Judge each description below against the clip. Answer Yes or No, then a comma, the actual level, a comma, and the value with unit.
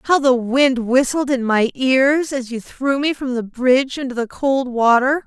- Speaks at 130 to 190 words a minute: No, fast, 205 wpm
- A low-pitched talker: No, very high, 260 Hz